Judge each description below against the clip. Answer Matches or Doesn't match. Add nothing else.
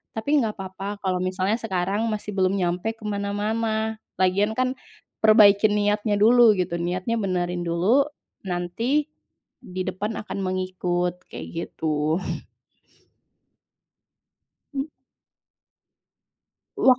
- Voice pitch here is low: Doesn't match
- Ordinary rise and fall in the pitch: Matches